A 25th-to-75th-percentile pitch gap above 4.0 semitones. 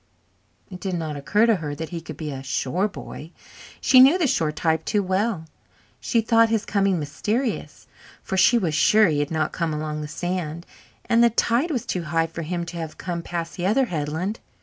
Yes: average, 5.3 semitones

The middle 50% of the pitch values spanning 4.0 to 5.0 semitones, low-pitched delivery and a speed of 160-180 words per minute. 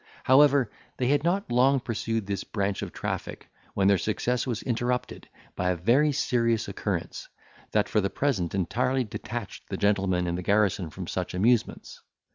Yes: average, 4.4 semitones; low, 110 Hz; average, 165 wpm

